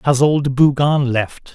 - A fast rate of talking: No, average, 155 wpm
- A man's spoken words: Yes, male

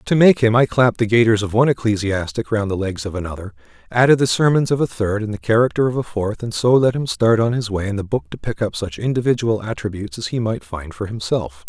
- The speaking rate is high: Yes, fast, 255 wpm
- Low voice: Yes, low, 110 Hz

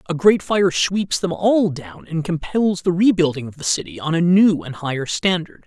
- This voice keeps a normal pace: No, fast, 210 wpm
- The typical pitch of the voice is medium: Yes, medium, 170 Hz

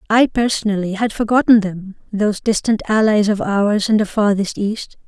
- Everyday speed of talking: Yes, average, 165 wpm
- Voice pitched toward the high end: Yes, high, 210 Hz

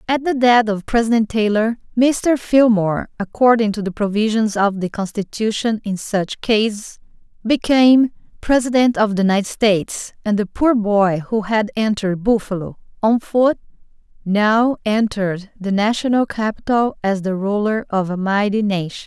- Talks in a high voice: Yes, high, 215 Hz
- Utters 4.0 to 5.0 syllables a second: Yes, 4.8 syllables/s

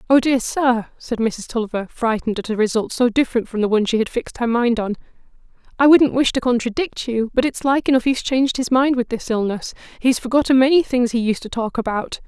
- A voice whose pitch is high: Yes, high, 240 Hz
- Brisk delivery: Yes, fast, 230 wpm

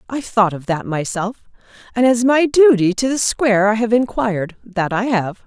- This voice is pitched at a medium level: No, high, 220 Hz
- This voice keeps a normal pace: Yes, average, 185 wpm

